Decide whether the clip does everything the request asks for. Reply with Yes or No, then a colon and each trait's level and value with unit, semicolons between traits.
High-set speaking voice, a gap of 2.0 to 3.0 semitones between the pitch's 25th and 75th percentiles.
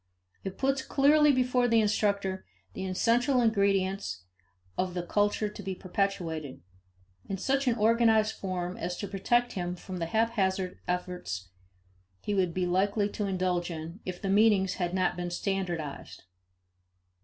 No: high, 195 Hz; average, 3.5 semitones